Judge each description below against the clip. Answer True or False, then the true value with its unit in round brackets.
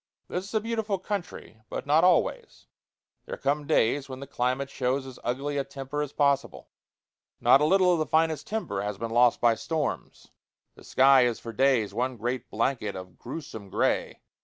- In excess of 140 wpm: True (185 wpm)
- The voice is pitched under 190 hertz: True (135 Hz)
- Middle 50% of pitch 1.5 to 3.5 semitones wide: False (4.3 semitones)